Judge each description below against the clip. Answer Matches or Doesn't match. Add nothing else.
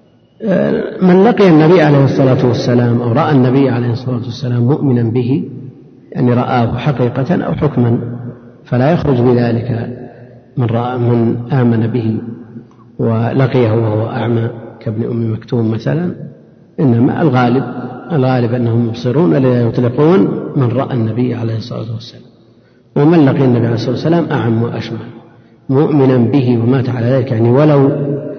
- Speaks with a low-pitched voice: Matches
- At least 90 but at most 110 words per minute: Doesn't match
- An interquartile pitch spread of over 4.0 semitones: Doesn't match